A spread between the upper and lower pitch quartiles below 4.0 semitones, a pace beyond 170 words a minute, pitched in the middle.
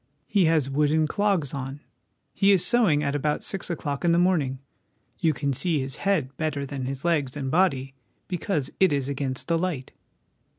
No: average, 4.3 semitones; average, 180 wpm; medium, 150 Hz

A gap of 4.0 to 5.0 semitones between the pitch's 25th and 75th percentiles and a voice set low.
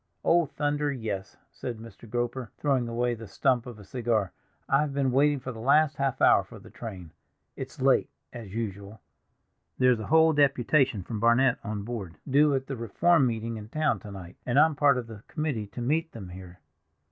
Yes: average, 4.3 semitones; low, 120 Hz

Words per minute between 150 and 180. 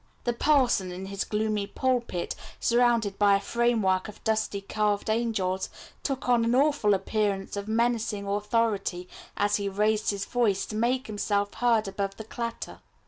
Yes: average, 155 wpm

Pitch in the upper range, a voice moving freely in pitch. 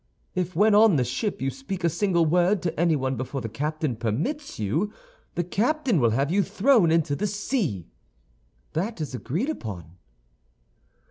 No: medium, 170 Hz; wide, 7.6 semitones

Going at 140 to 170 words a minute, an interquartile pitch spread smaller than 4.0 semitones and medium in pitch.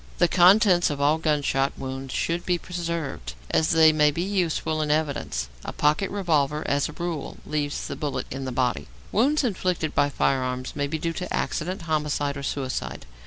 No: average, 180 wpm; average, 3.6 semitones; medium, 155 Hz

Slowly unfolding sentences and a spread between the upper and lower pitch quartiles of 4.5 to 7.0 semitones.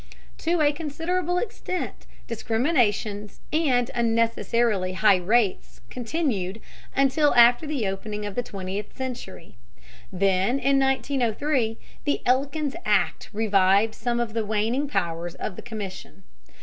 Yes: slow, 120 wpm; average, 5.0 semitones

